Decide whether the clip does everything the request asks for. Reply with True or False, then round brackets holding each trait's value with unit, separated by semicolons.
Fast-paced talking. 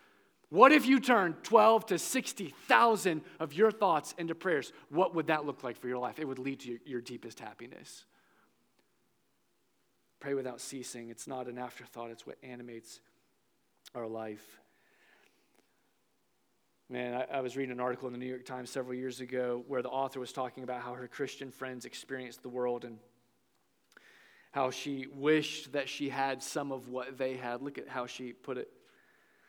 False (175 wpm)